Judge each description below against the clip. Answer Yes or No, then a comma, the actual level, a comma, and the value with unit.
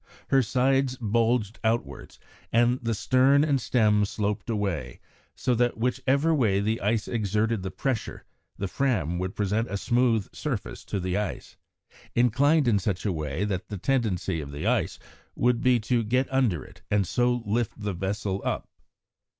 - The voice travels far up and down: No, average, 3.9 semitones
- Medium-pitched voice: No, low, 110 Hz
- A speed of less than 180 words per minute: Yes, average, 165 wpm